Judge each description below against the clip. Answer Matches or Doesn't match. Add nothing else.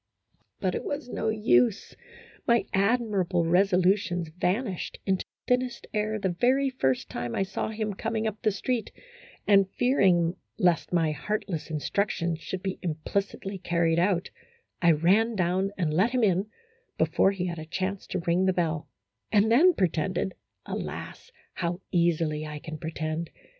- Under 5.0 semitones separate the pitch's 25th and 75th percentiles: Matches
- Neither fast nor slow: Matches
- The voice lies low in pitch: Doesn't match